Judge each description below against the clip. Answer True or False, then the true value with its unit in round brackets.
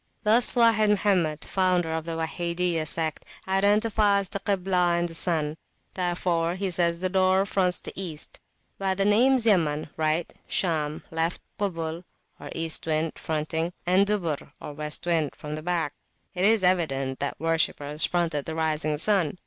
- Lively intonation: False (3.3 semitones)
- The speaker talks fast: False (170 wpm)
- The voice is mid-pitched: True (170 Hz)